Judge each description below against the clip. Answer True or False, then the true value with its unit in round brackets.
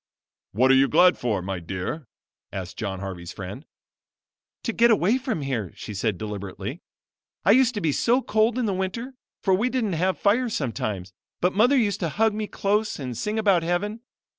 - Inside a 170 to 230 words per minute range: True (190 wpm)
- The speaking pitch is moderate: True (180 Hz)